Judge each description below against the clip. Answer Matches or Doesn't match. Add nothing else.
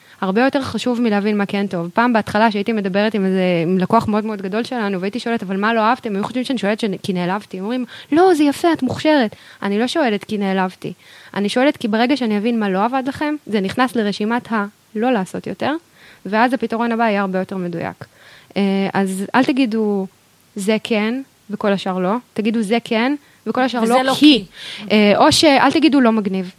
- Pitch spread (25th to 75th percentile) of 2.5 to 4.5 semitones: Matches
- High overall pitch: Matches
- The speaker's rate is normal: Doesn't match